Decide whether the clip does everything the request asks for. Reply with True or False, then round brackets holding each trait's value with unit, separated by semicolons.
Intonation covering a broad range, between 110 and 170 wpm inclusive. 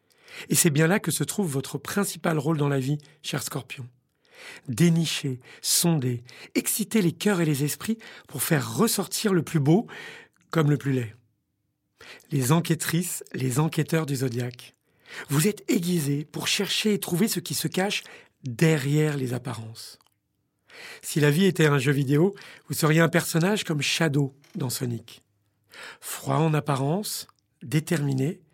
False (4.1 semitones; 150 wpm)